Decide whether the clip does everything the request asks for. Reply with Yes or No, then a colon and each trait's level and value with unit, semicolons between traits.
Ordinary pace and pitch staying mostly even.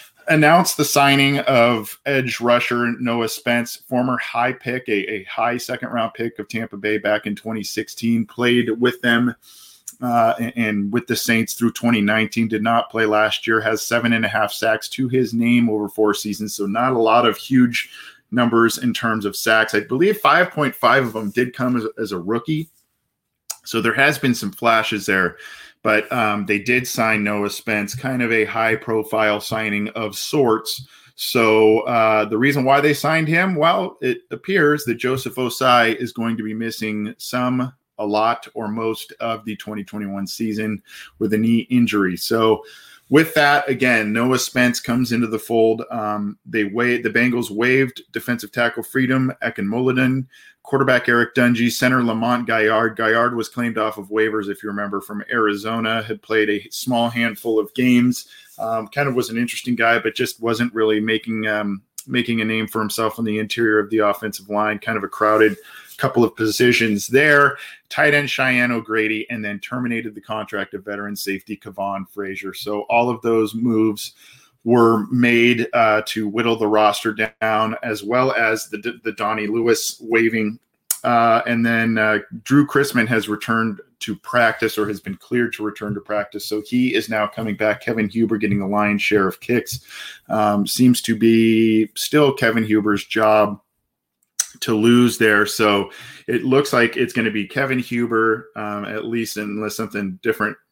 Yes: average, 175 wpm; narrow, 2.3 semitones